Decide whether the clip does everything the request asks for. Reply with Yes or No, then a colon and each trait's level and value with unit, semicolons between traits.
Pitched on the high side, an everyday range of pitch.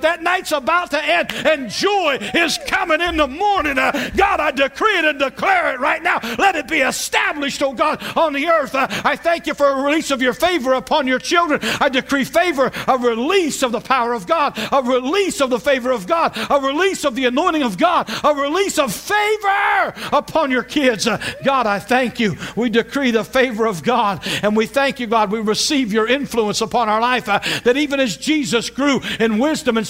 Yes: very high, 275 Hz; average, 4.8 semitones